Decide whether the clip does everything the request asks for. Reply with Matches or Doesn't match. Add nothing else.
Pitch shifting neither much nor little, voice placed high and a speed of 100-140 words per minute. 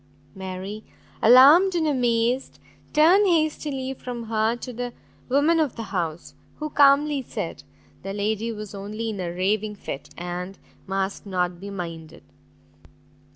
Doesn't match